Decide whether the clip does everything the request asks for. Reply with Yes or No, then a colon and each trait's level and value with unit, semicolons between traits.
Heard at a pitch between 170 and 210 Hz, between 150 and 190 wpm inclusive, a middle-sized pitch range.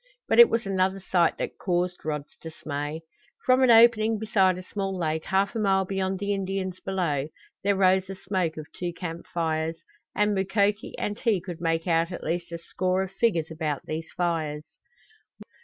Yes: medium, 185 Hz; average, 180 wpm; average, 3.1 semitones